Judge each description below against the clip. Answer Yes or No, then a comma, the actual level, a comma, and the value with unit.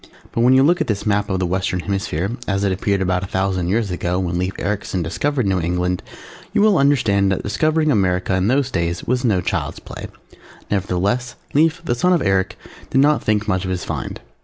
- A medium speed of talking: No, fast, 210 wpm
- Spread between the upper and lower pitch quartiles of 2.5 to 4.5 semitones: No, average, 5.2 semitones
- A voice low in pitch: Yes, low, 100 Hz